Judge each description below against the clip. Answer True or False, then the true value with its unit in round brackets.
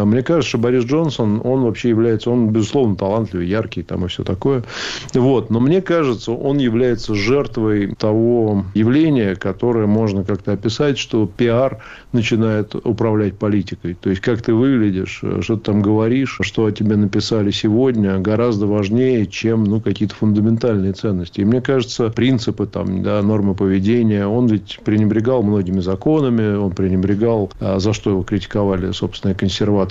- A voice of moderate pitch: False (110 Hz)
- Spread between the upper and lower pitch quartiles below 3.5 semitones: True (2.9 semitones)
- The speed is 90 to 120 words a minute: False (155 wpm)